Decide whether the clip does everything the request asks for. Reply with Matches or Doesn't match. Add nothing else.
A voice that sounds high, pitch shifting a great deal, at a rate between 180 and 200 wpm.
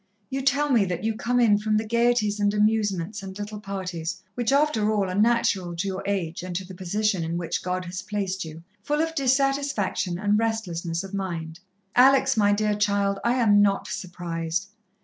Doesn't match